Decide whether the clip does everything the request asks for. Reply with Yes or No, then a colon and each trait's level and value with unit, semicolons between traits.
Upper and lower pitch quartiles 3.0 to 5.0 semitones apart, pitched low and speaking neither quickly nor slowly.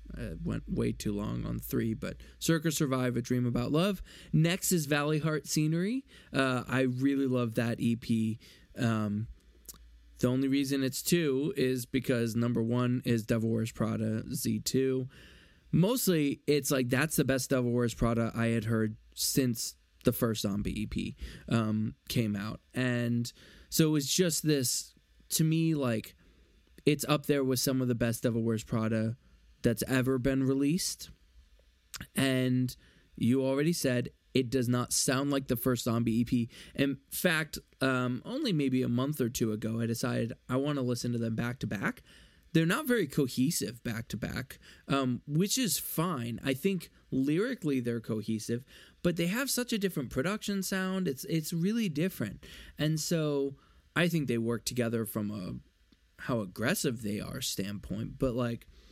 Yes: average, 4.3 semitones; low, 125 Hz; average, 165 wpm